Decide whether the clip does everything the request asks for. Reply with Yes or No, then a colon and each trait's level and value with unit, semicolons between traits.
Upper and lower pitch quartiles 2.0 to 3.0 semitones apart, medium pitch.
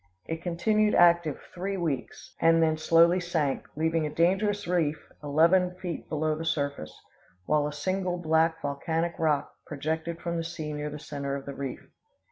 Yes: narrow, 2.6 semitones; medium, 160 Hz